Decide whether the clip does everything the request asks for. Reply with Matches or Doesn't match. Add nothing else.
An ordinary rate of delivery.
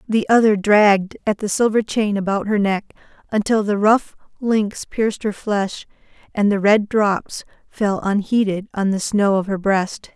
Matches